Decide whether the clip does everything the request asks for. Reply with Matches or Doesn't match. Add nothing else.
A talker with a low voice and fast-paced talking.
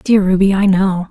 Doesn't match